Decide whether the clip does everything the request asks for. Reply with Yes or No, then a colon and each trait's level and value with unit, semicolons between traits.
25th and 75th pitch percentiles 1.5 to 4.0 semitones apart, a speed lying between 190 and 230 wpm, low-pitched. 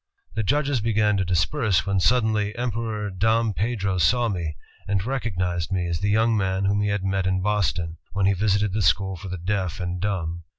Yes: average, 2.9 semitones; average, 200 wpm; low, 100 Hz